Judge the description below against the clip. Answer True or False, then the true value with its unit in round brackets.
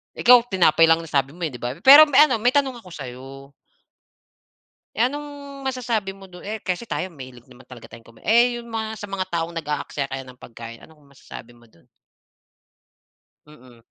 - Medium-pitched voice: True (165 Hz)